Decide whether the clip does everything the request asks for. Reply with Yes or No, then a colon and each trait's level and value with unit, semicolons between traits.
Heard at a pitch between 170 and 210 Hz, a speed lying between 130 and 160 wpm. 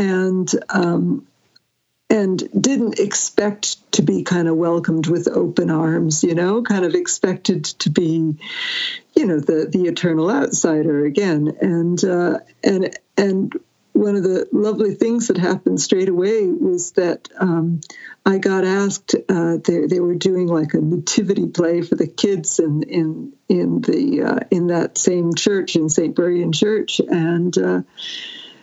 Yes: medium, 185 Hz; average, 155 wpm